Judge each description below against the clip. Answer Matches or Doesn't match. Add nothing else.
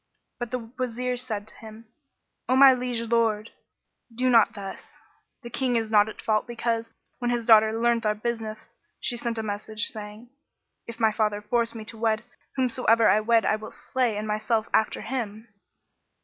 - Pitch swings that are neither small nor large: Doesn't match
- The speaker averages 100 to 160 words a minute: Doesn't match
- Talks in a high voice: Matches